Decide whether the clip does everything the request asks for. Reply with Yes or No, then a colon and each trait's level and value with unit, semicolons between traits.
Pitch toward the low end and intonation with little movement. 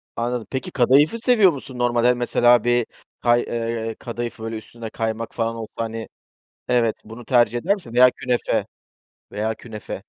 Yes: low, 120 Hz; narrow, 1.5 semitones